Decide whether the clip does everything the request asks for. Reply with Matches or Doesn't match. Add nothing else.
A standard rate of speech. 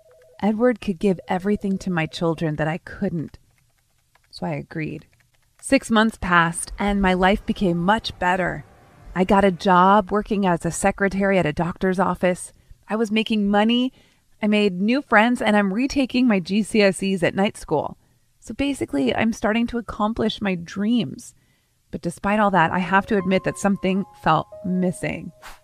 Matches